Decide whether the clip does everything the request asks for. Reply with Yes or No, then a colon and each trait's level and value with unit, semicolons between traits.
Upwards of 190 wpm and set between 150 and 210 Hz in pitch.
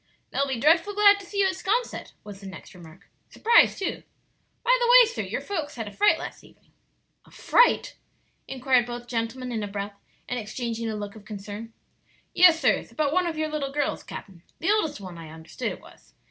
No: fast, 205 wpm; very high, 255 Hz